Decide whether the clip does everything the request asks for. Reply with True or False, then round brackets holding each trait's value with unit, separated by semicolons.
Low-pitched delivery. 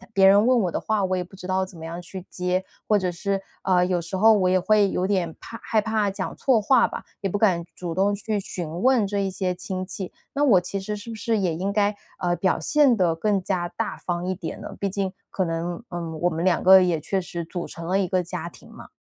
False (190 Hz)